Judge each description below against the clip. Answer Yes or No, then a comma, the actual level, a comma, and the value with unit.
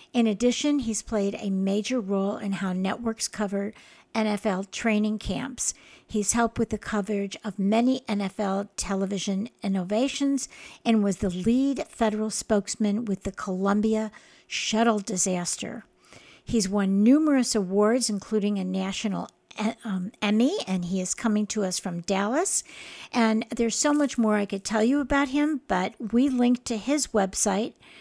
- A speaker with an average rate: Yes, average, 150 wpm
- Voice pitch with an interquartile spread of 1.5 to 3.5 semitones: Yes, average, 2.9 semitones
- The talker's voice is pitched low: No, high, 215 Hz